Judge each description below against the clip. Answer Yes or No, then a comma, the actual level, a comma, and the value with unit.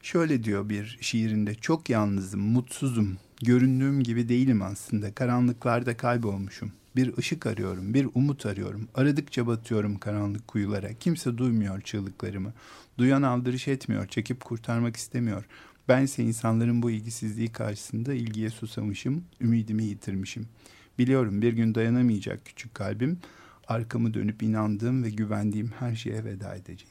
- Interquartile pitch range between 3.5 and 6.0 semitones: No, average, 2.9 semitones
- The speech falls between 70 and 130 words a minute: Yes, average, 125 wpm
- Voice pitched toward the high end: No, low, 115 Hz